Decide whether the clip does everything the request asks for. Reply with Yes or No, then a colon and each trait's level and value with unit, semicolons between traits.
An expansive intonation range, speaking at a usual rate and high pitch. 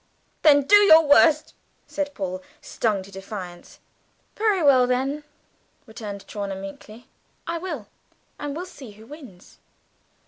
No: wide, 7.1 semitones; slow, 130 wpm; very high, 260 Hz